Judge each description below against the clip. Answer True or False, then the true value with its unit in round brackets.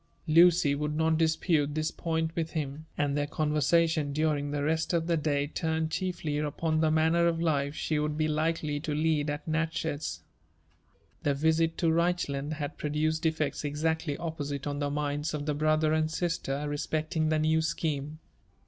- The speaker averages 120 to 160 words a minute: False (175 wpm)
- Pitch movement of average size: False (1.6 semitones)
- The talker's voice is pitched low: False (155 Hz)